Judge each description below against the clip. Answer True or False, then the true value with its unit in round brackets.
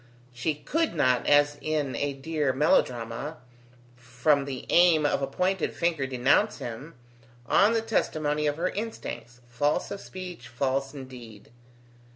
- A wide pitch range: False (4.4 semitones)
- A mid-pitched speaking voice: True (145 Hz)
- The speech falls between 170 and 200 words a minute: False (145 wpm)